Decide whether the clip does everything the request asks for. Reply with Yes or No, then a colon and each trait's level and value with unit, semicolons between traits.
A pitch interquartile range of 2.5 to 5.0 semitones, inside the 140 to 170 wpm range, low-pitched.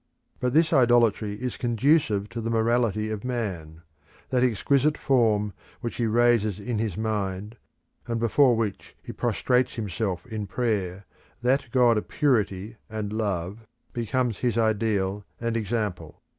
Yes: average, 2.8 semitones; average, 145 wpm; low, 110 Hz